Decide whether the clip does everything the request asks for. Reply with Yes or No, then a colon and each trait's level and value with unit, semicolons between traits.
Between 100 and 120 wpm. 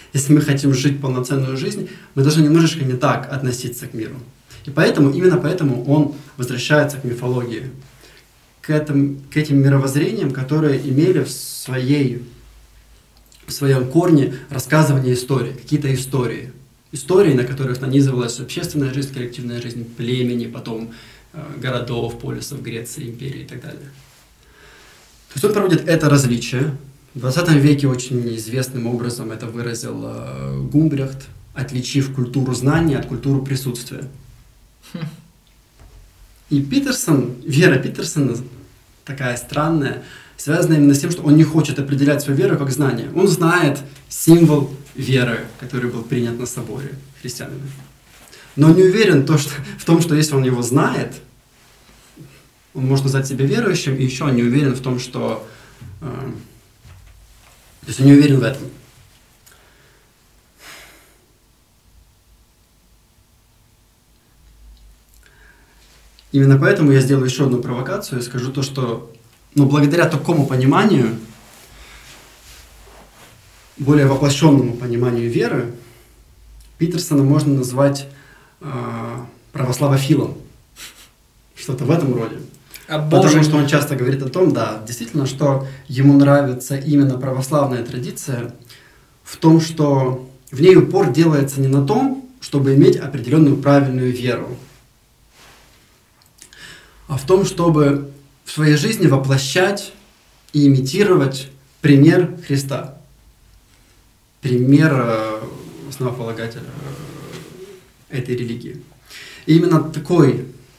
Yes: average, 115 wpm